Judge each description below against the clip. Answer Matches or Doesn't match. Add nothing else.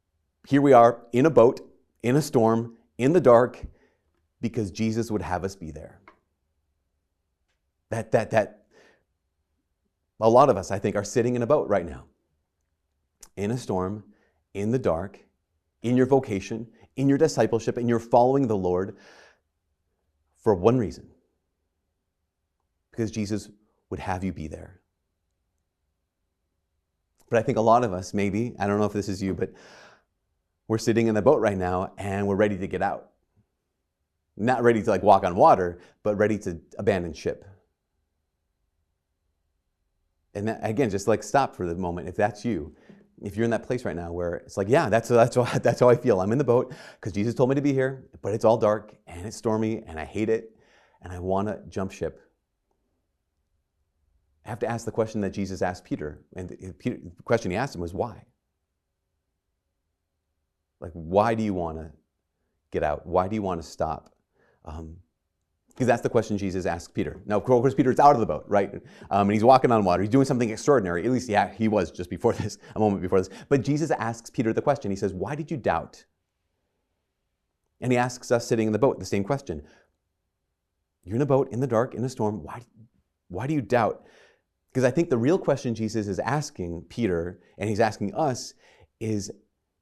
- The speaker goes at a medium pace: Matches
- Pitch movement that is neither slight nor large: Doesn't match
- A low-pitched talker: Matches